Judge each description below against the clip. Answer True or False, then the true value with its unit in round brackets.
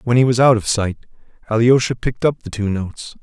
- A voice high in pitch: False (115 Hz)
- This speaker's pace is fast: True (225 wpm)